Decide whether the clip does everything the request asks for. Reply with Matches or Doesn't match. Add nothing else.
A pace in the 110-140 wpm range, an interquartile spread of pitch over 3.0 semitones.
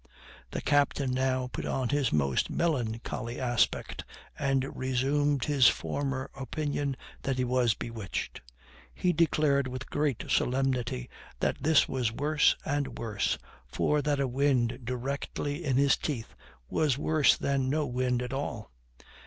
Doesn't match